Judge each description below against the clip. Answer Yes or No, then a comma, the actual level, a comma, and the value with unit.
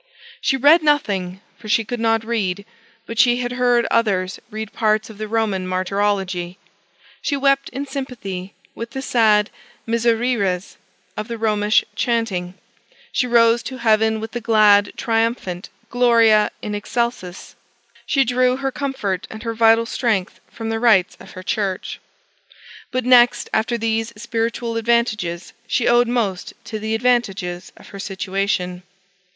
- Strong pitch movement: No, average, 3.1 semitones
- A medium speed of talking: Yes, average, 145 wpm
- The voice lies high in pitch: Yes, high, 225 Hz